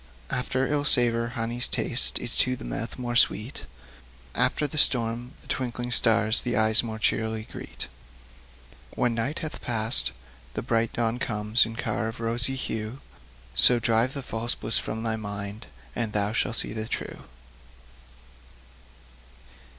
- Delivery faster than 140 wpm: Yes, average, 150 wpm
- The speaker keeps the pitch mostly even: Yes, narrow, 1.7 semitones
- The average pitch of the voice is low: Yes, low, 115 Hz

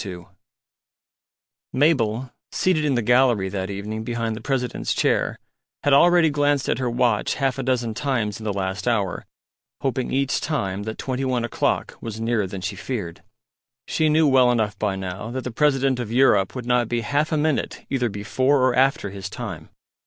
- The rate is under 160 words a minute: No, average, 180 wpm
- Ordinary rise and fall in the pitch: Yes, average, 4.3 semitones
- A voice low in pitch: Yes, low, 120 Hz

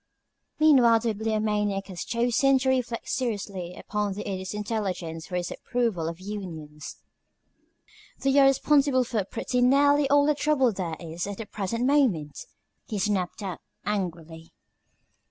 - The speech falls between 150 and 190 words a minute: No, average, 140 wpm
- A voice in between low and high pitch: No, high, 210 Hz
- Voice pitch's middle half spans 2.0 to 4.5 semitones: No, wide, 5.6 semitones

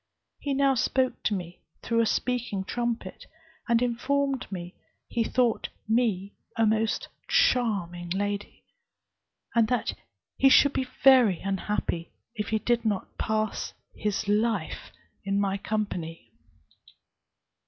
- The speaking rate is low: Yes, slow, 120 wpm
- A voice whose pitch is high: Yes, high, 220 Hz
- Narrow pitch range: No, average, 3.6 semitones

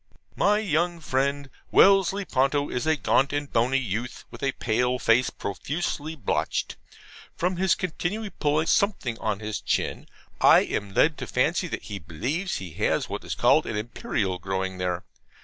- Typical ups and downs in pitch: No, wide, 7.7 semitones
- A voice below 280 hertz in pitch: Yes, low, 135 Hz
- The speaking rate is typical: Yes, average, 165 wpm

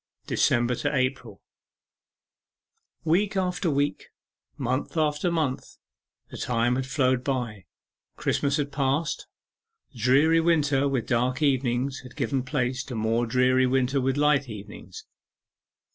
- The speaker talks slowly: Yes, slow, 120 wpm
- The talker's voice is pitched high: No, low, 130 Hz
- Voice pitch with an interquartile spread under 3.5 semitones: Yes, average, 2.8 semitones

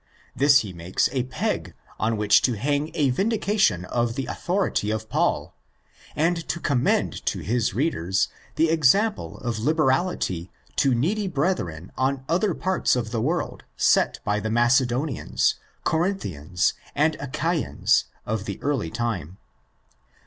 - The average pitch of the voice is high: No, low, 130 Hz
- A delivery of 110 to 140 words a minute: Yes, slow, 135 wpm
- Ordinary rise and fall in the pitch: No, wide, 6.7 semitones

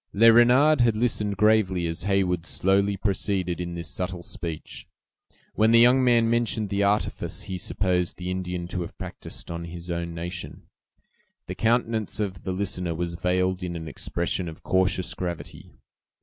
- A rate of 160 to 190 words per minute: Yes, average, 165 wpm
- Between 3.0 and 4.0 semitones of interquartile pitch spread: Yes, average, 3.5 semitones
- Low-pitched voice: Yes, very low, 95 Hz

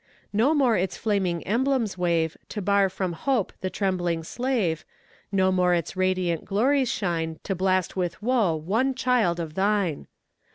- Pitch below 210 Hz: Yes, high, 190 Hz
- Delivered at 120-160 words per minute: Yes, average, 155 wpm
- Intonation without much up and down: No, average, 4.4 semitones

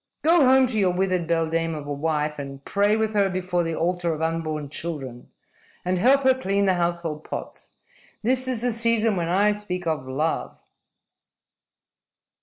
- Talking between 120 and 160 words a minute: No, average, 170 wpm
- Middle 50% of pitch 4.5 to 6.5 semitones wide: Yes, average, 4.9 semitones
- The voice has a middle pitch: Yes, medium, 180 Hz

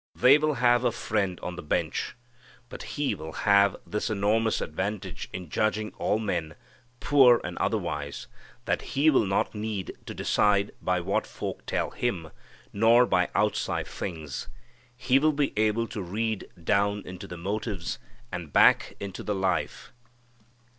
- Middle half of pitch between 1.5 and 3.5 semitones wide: No, average, 3.9 semitones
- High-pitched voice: No, low, 105 Hz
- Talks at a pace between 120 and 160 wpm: Yes, average, 155 wpm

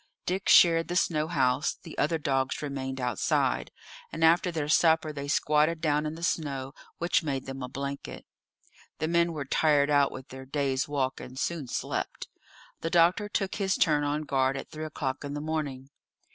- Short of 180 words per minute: No, average, 185 wpm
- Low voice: No, medium, 150 Hz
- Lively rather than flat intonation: No, average, 3.2 semitones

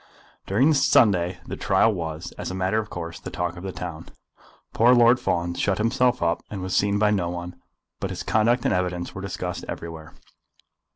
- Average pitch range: Yes, average, 3.8 semitones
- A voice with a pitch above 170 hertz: No, very low, 95 Hz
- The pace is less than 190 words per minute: No, average, 195 wpm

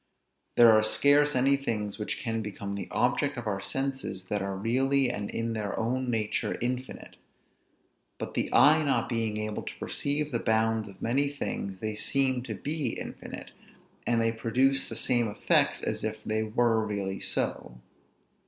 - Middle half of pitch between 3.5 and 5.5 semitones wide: Yes, average, 3.9 semitones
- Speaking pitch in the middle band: No, low, 115 Hz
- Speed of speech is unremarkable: Yes, average, 170 wpm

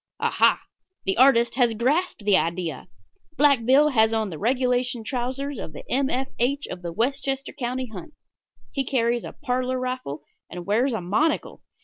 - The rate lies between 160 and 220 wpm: Yes, average, 165 wpm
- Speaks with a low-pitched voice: No, high, 245 Hz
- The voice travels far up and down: No, average, 3.5 semitones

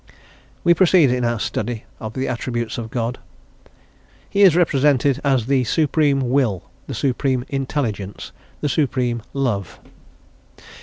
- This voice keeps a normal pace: No, slow, 125 wpm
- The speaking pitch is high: No, low, 130 Hz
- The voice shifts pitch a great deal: No, average, 3.3 semitones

